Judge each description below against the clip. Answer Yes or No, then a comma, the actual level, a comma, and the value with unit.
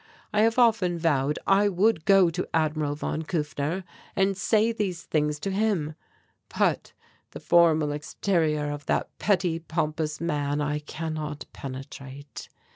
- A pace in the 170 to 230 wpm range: No, slow, 135 wpm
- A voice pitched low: No, medium, 160 Hz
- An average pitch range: Yes, average, 4.4 semitones